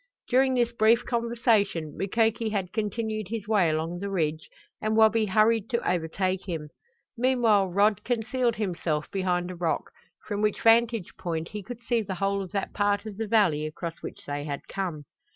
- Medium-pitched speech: No, high, 205 Hz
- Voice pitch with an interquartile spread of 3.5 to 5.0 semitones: Yes, average, 4.1 semitones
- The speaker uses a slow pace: No, average, 175 wpm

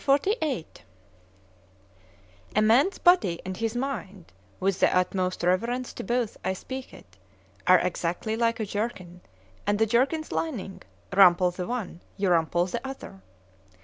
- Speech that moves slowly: Yes, slow, 130 wpm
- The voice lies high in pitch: Yes, high, 205 Hz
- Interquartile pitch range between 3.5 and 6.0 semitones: Yes, average, 5.3 semitones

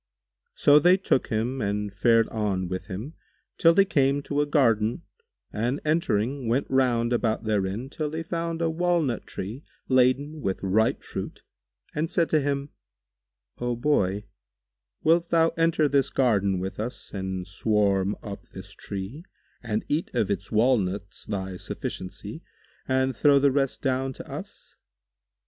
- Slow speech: No, average, 150 wpm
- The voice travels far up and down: Yes, wide, 6.1 semitones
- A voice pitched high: No, low, 125 Hz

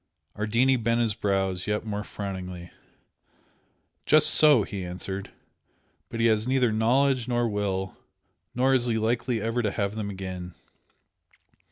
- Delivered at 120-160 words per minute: Yes, average, 140 wpm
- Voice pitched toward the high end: No, low, 110 Hz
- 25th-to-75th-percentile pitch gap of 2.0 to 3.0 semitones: No, average, 3.6 semitones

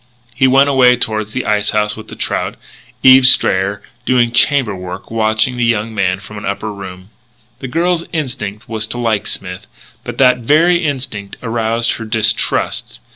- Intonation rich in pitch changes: No, average, 3.6 semitones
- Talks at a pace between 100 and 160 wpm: No, average, 170 wpm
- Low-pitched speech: Yes, low, 115 Hz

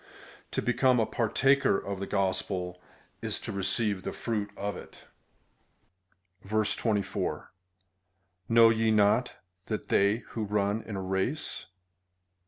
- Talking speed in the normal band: No, slow, 120 wpm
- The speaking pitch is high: No, low, 105 Hz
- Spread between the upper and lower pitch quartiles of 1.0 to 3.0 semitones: Yes, narrow, 2.5 semitones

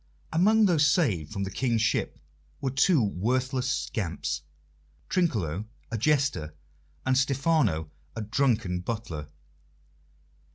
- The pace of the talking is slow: Yes, slow, 110 wpm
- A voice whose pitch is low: Yes, low, 120 Hz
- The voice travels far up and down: Yes, wide, 7.1 semitones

